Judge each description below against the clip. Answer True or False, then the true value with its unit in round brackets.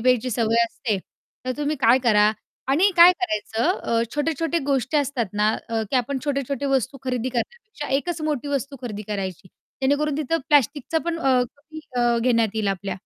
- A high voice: True (260 Hz)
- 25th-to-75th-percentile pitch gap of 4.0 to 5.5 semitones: True (4.3 semitones)